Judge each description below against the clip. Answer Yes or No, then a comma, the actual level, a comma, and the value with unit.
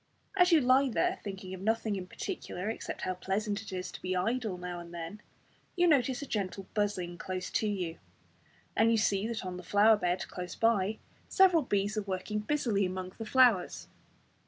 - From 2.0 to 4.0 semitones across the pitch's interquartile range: Yes, average, 3.6 semitones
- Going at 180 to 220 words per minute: Yes, average, 190 wpm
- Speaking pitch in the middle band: No, high, 205 Hz